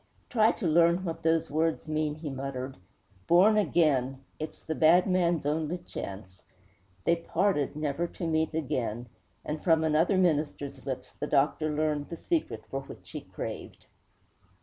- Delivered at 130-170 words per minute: Yes, average, 150 wpm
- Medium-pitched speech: Yes, medium, 155 Hz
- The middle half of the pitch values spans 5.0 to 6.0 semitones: No, average, 3.3 semitones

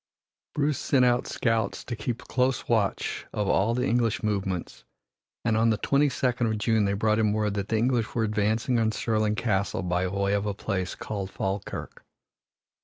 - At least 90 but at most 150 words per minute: No, average, 180 wpm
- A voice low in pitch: Yes, low, 110 Hz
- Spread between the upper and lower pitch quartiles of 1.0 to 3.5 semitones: Yes, average, 2.8 semitones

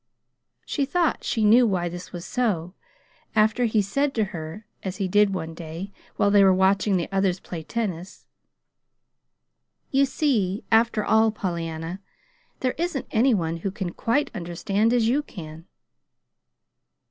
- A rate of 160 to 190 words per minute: No, average, 150 wpm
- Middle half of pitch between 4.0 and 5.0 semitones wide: Yes, average, 4.6 semitones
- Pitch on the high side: Yes, high, 200 Hz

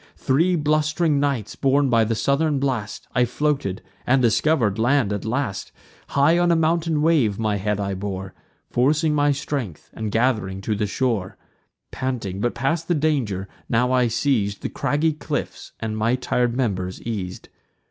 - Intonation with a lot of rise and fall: Yes, wide, 5.7 semitones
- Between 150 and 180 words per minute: Yes, average, 160 wpm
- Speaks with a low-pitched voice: Yes, low, 125 Hz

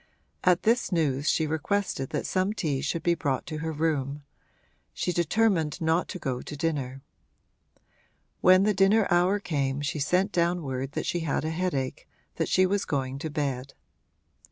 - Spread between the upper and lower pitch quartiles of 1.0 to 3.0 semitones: No, average, 4.6 semitones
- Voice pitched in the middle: Yes, medium, 160 Hz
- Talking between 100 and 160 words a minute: No, average, 170 wpm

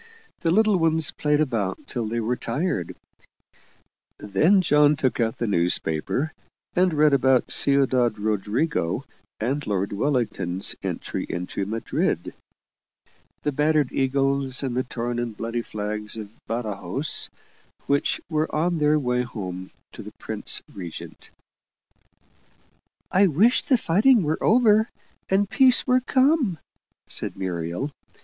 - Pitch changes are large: Yes, wide, 6.8 semitones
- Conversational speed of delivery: No, slow, 125 wpm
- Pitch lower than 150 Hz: Yes, low, 135 Hz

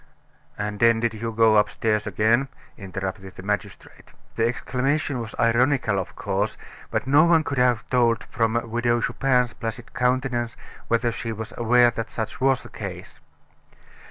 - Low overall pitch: Yes, low, 115 Hz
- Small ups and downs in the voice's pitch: Yes, narrow, 2.2 semitones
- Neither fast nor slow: Yes, average, 155 wpm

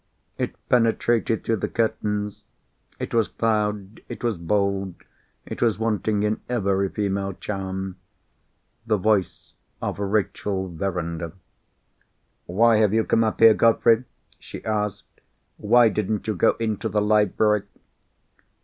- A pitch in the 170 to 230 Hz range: No, low, 105 Hz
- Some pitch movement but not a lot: No, narrow, 2.3 semitones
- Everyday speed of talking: No, slow, 125 wpm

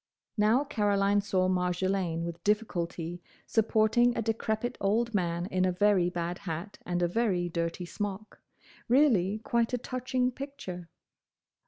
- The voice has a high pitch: Yes, high, 200 Hz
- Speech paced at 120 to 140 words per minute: Yes, slow, 135 wpm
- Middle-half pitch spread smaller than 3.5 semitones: No, average, 4.3 semitones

